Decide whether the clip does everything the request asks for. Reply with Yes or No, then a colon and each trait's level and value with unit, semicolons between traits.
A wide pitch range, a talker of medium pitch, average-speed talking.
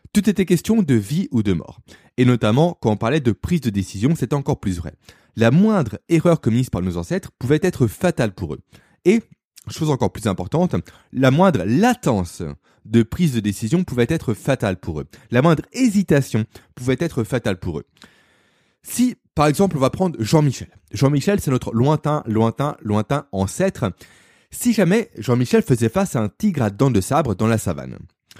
No: wide, 7.5 semitones; low, 125 Hz; average, 185 wpm